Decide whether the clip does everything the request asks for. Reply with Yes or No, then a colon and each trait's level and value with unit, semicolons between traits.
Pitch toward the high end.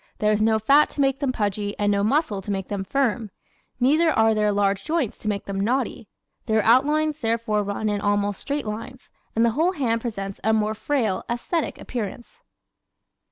Yes: high, 220 Hz